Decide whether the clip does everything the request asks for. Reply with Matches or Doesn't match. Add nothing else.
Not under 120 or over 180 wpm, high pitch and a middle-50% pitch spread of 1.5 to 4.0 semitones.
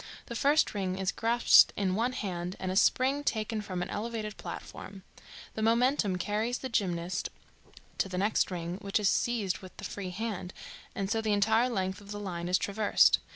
Doesn't match